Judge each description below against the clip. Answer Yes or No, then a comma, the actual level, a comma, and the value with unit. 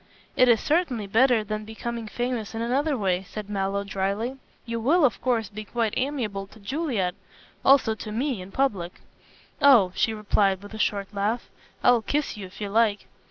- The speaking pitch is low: No, high, 220 Hz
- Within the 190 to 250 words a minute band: No, average, 180 wpm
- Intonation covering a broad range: No, average, 3.7 semitones